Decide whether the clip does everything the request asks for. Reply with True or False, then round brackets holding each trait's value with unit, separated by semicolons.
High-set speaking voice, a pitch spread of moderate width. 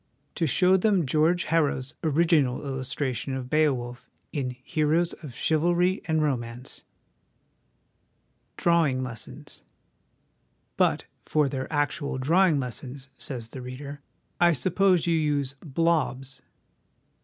False (145 Hz; 4.2 semitones)